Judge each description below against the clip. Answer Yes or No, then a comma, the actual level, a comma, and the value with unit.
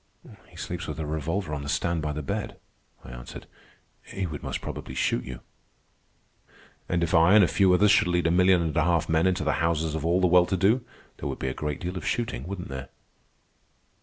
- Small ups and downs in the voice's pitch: No, average, 3.1 semitones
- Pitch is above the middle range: No, very low, 85 Hz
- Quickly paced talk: Yes, fast, 230 wpm